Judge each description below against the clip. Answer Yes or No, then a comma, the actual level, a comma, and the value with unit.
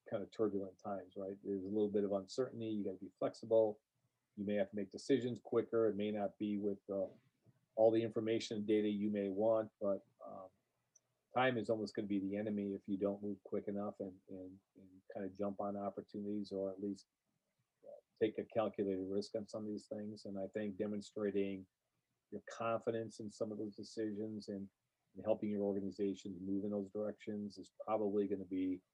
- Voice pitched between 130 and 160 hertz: No, low, 105 Hz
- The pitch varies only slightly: Yes, narrow, 1.5 semitones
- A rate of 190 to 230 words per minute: Yes, fast, 205 wpm